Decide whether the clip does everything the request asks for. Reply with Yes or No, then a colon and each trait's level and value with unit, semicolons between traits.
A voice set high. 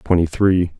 No: very low, 90 Hz